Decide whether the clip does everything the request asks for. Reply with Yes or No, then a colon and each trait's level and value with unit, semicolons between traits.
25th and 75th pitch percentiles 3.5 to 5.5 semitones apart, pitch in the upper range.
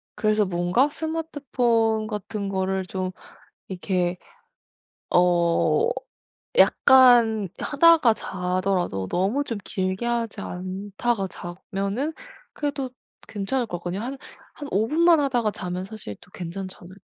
Yes: average, 5.2 semitones; high, 205 Hz